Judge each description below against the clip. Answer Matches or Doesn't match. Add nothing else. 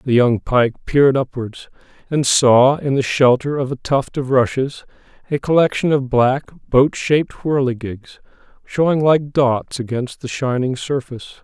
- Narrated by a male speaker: Matches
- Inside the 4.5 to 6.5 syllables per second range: Doesn't match